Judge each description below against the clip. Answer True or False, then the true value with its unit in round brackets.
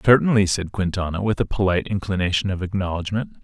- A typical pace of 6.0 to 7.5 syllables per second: True (6.4 syllables/s)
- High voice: False (95 Hz)